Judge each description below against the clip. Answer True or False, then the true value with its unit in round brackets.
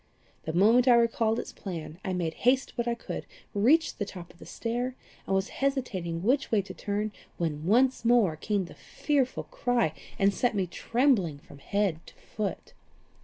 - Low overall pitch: False (210 Hz)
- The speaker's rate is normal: True (180 wpm)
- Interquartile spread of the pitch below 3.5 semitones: False (5.2 semitones)